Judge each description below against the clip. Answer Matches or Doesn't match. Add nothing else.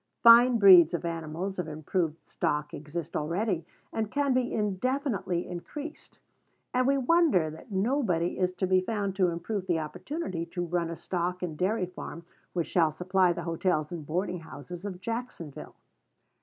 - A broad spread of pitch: Doesn't match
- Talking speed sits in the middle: Matches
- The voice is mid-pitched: Matches